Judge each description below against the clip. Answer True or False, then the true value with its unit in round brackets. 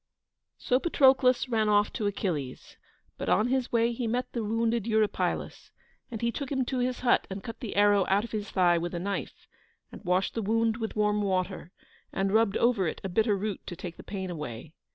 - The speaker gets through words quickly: True (210 wpm)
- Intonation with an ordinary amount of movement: True (3.5 semitones)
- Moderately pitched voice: False (210 Hz)